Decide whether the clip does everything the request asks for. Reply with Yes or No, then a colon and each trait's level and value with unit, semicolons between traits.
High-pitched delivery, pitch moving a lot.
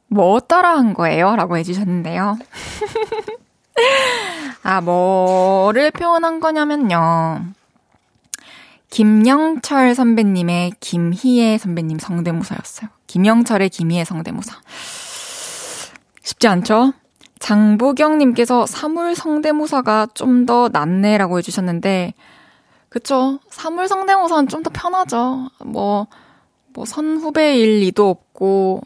Yes: high, 235 Hz; wide, 8.2 semitones